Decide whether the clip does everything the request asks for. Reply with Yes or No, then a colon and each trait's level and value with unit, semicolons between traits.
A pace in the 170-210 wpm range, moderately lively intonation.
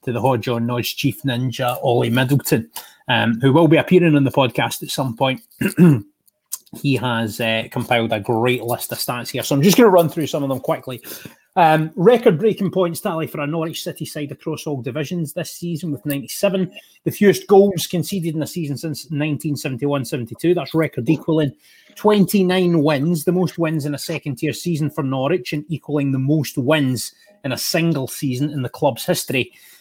Yes: average, 190 wpm; average, 4.0 semitones